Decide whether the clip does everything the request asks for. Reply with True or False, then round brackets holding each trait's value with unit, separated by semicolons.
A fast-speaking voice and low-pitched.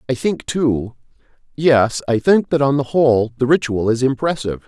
False (165 wpm; 130 Hz)